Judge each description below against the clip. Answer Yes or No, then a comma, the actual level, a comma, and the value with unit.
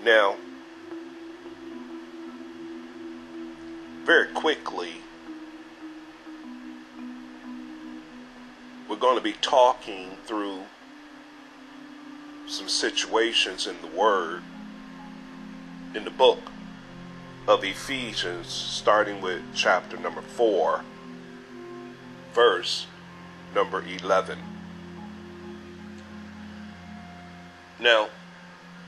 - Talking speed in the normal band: No, slow, 60 wpm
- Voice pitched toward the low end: Yes, low, 100 Hz